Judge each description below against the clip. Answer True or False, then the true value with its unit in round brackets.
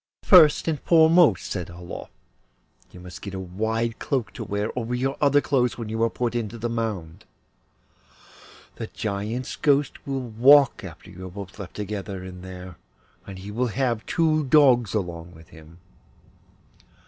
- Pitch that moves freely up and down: True (5.7 semitones)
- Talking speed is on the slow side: False (160 wpm)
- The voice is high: False (110 Hz)